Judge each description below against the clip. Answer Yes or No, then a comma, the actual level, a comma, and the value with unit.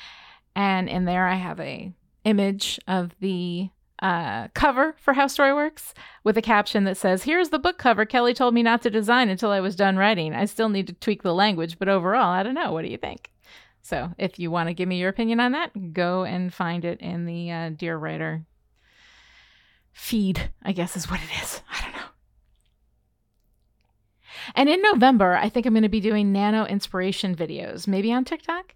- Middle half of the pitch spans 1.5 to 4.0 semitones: No, average, 4.5 semitones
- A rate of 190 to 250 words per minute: Yes, average, 200 wpm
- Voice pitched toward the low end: No, high, 195 Hz